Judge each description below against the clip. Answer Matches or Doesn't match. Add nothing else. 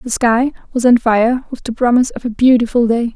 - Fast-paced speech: Matches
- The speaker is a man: Doesn't match